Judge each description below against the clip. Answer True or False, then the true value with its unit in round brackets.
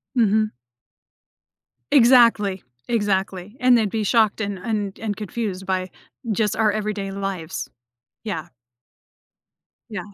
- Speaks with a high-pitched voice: True (210 Hz)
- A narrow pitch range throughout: True (2.3 semitones)